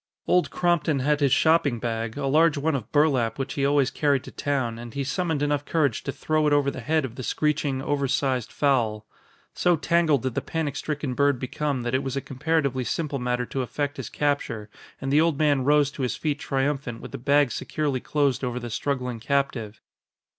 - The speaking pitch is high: No, medium, 140 Hz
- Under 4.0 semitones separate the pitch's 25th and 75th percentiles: Yes, average, 2.7 semitones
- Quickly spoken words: Yes, fast, 210 wpm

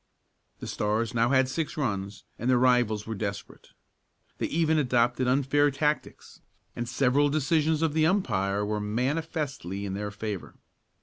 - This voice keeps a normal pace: Yes, average, 145 wpm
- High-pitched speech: No, low, 125 Hz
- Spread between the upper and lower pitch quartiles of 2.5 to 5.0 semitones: No, wide, 5.6 semitones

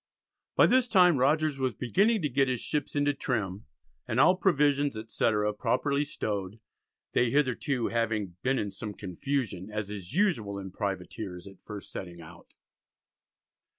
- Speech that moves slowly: No, average, 150 wpm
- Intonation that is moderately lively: No, wide, 6.2 semitones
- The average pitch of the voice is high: No, low, 115 Hz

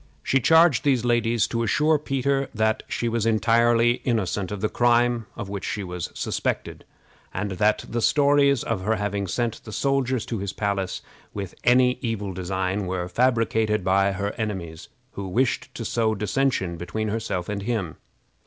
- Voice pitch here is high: No, low, 110 Hz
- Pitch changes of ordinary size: Yes, average, 3.6 semitones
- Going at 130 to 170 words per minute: Yes, average, 165 wpm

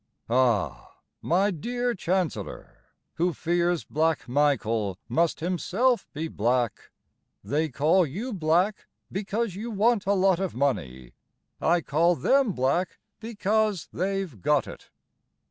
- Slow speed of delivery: Yes, slow, 120 wpm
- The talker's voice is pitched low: No, medium, 175 Hz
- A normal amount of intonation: No, wide, 5.7 semitones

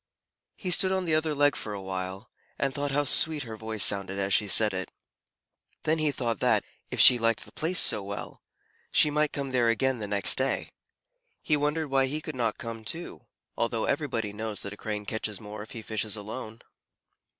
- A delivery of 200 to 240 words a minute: Yes, fast, 205 wpm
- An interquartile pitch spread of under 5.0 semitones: No, wide, 5.6 semitones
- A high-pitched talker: No, low, 115 Hz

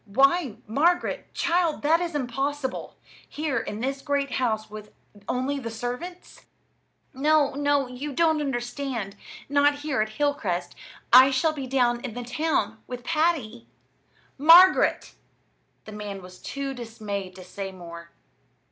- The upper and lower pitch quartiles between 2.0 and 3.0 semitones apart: No, average, 4.8 semitones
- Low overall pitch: No, very high, 265 Hz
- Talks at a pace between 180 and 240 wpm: No, slow, 135 wpm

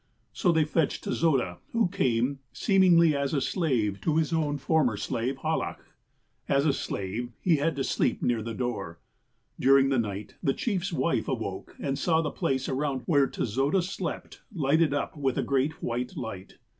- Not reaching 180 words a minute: Yes, average, 170 wpm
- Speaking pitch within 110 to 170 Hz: Yes, medium, 140 Hz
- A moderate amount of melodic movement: Yes, average, 4.6 semitones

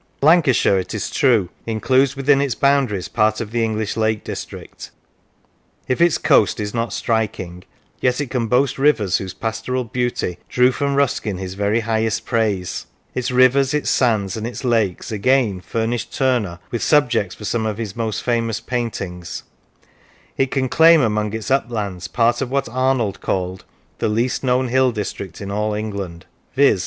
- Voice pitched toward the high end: No, low, 115 Hz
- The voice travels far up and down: No, average, 3.7 semitones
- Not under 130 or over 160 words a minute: No, average, 170 wpm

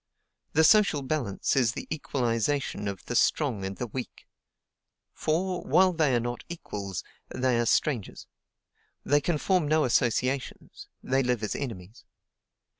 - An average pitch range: Yes, average, 5.0 semitones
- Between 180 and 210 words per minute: No, average, 140 wpm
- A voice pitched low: Yes, low, 130 Hz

